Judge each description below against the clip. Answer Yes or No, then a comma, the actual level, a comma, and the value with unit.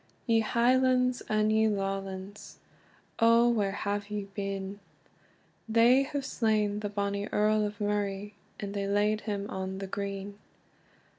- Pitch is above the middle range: Yes, high, 205 Hz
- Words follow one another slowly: Yes, slow, 130 wpm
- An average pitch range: No, narrow, 1.6 semitones